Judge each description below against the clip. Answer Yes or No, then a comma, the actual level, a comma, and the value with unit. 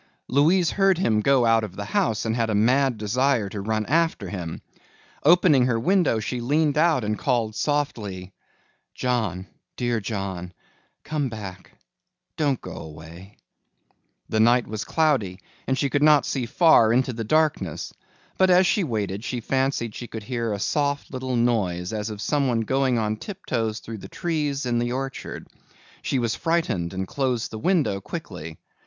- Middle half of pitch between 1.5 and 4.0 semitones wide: No, average, 5.0 semitones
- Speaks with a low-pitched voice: Yes, low, 120 Hz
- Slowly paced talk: No, average, 165 wpm